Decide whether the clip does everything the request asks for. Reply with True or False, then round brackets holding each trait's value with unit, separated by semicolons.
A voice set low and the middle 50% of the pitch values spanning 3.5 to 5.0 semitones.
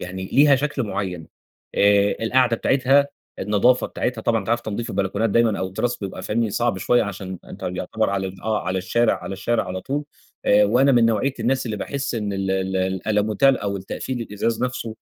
True (110 Hz; 3.9 semitones)